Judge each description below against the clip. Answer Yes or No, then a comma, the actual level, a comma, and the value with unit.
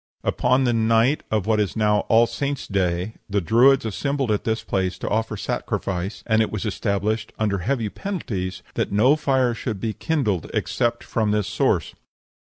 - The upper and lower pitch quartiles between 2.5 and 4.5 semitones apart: Yes, average, 3.2 semitones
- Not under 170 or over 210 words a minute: Yes, average, 175 wpm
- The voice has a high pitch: No, low, 110 Hz